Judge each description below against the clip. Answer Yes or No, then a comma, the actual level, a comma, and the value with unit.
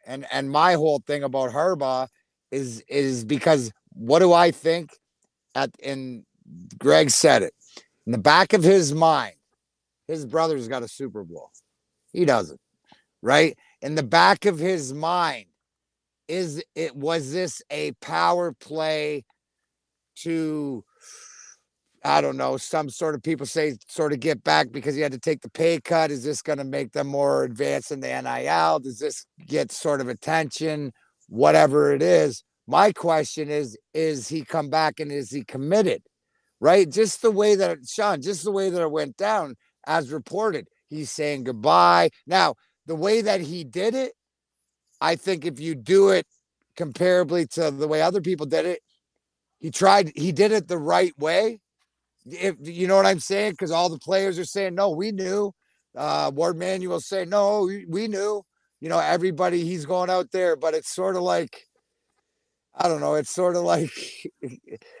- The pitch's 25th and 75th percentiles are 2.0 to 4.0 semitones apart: No, average, 4.9 semitones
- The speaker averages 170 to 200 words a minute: Yes, average, 175 wpm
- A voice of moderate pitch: Yes, medium, 160 Hz